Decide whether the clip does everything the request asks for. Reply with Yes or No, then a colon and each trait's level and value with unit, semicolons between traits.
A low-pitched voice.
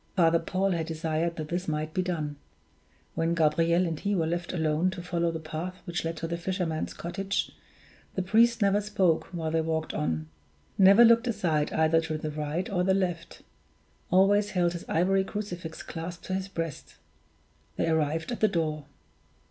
No: medium, 170 Hz